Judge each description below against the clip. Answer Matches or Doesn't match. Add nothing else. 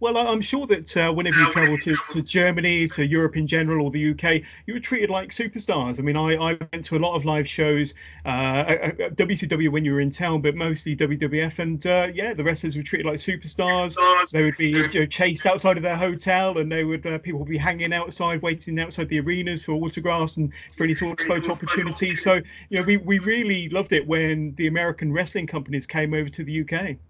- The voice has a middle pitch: Matches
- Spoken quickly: Matches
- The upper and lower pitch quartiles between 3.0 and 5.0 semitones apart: Doesn't match